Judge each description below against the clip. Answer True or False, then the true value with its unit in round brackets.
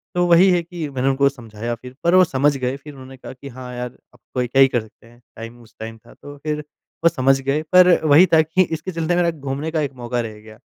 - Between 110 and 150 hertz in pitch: True (135 Hz)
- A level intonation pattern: False (4.6 semitones)